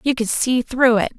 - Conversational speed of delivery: No, fast, 255 wpm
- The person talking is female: Yes, female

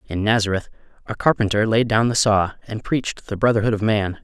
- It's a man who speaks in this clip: Yes, male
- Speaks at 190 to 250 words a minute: Yes, average, 200 wpm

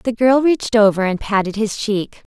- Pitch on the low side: No, high, 220 Hz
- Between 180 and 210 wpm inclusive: Yes, average, 200 wpm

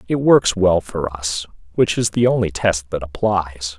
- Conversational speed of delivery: Yes, average, 190 wpm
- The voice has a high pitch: No, very low, 95 Hz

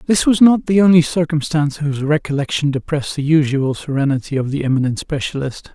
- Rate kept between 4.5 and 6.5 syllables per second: Yes, 6.1 syllables/s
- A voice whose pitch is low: No, medium, 150 Hz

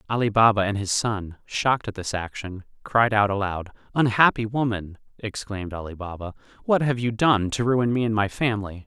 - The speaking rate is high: No, average, 185 wpm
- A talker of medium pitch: No, low, 105 Hz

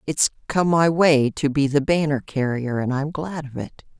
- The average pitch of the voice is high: No, medium, 145 Hz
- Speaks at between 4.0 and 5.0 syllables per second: Yes, 4.5 syllables/s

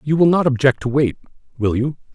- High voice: No, low, 135 Hz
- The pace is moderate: No, fast, 225 wpm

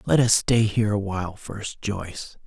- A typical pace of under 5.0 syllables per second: Yes, 4.7 syllables/s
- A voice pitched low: Yes, low, 105 Hz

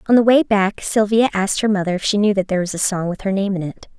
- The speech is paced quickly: Yes, fast, 315 wpm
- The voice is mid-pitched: No, high, 200 Hz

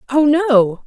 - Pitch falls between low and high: No, very high, 250 Hz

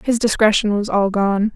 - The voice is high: Yes, high, 210 Hz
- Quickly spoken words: No, average, 195 wpm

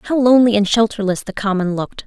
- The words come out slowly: No, fast, 205 wpm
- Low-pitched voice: No, high, 210 Hz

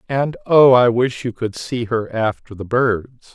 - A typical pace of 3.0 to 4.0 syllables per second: Yes, 3.9 syllables/s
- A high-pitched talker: No, low, 120 Hz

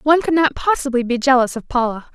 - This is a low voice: No, very high, 265 Hz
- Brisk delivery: Yes, fast, 225 wpm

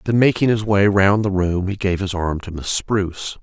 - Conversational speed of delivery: No, fast, 245 wpm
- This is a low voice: Yes, very low, 95 Hz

